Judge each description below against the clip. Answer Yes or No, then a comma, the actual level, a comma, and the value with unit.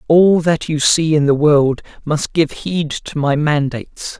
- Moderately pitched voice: Yes, medium, 150 Hz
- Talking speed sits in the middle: Yes, average, 185 wpm